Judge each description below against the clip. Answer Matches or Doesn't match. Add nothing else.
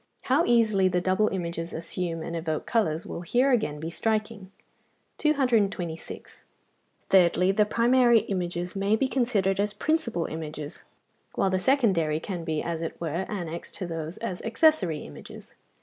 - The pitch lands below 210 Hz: Matches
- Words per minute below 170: Matches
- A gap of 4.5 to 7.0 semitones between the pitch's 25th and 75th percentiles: Matches